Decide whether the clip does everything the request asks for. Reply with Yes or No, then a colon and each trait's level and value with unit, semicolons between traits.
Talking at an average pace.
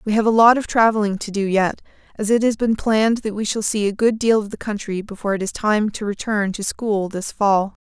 No: fast, 260 wpm